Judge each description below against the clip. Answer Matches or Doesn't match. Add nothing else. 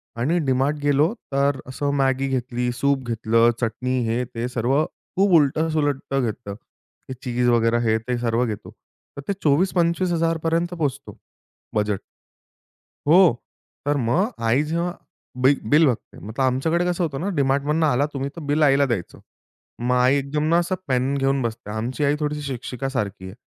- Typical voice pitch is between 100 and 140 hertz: Matches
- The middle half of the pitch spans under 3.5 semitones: Doesn't match